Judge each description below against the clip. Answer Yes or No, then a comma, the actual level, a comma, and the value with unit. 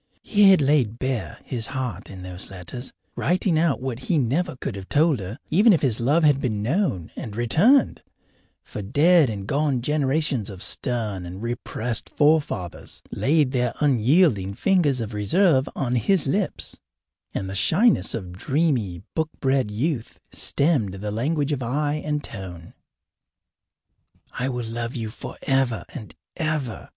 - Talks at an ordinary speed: Yes, average, 150 wpm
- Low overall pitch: Yes, low, 130 Hz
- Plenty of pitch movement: Yes, wide, 6.1 semitones